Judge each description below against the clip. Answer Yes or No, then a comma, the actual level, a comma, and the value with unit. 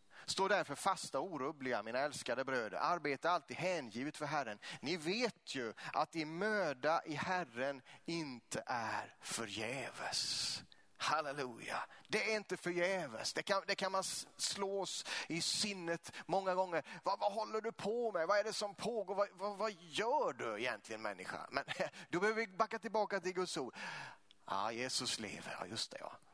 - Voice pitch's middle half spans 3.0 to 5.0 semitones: Yes, average, 4.4 semitones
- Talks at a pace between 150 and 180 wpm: Yes, average, 165 wpm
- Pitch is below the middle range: No, medium, 185 Hz